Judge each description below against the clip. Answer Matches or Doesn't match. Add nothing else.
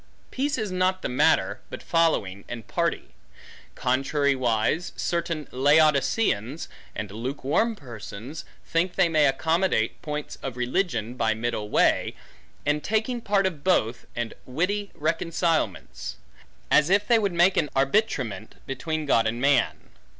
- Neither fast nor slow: Doesn't match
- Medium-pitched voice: Matches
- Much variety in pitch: Matches